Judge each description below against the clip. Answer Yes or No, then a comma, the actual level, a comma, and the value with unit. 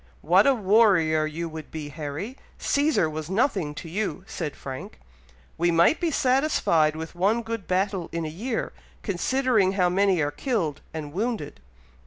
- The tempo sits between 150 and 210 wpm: Yes, average, 160 wpm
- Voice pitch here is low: No, medium, 180 Hz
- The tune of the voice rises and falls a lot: Yes, wide, 6.0 semitones